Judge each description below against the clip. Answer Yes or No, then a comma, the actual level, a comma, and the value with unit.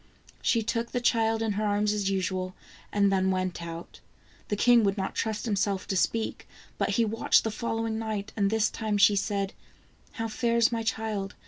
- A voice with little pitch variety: Yes, narrow, 2.3 semitones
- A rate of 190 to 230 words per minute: Yes, average, 195 wpm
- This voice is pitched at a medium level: No, high, 210 Hz